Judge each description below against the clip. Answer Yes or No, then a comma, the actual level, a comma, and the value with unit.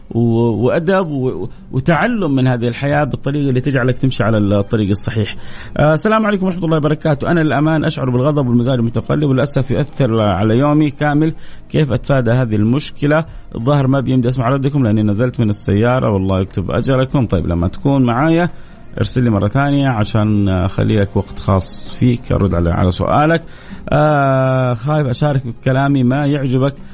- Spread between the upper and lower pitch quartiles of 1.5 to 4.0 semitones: No, average, 4.4 semitones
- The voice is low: Yes, low, 130 Hz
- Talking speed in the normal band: No, fast, 150 wpm